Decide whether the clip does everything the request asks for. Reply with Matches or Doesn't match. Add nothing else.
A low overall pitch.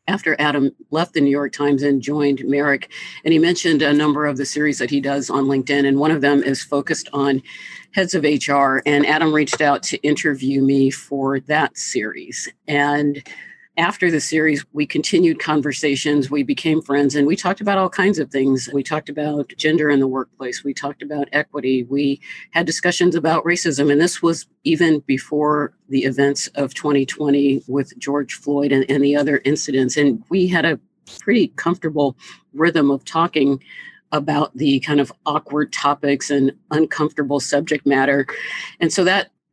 Doesn't match